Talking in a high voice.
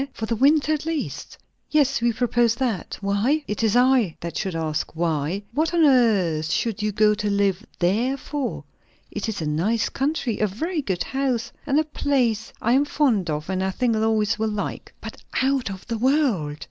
Yes: high, 225 Hz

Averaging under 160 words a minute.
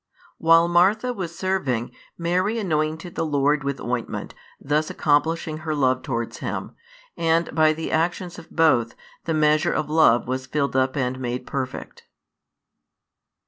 Yes: average, 140 wpm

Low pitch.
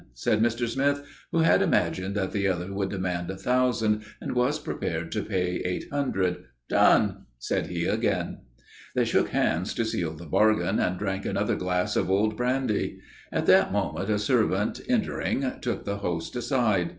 Yes: low, 100 Hz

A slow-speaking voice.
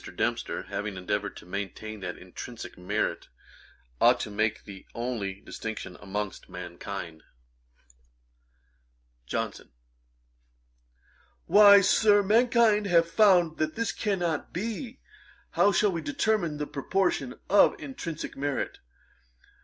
Yes: slow, 105 wpm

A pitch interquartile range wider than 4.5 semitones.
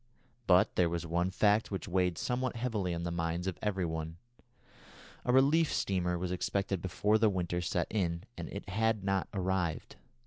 No: average, 3.2 semitones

